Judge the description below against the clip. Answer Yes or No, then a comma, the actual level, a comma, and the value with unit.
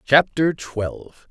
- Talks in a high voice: No, low, 135 Hz